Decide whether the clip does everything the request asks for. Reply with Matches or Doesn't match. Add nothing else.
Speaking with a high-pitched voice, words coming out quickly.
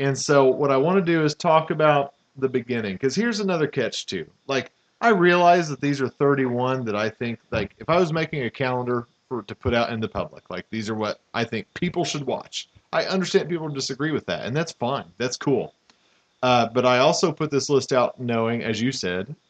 Doesn't match